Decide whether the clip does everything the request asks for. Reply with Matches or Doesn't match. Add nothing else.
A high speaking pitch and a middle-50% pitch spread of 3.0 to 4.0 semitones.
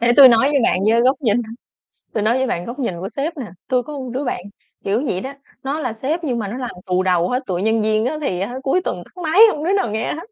Doesn't match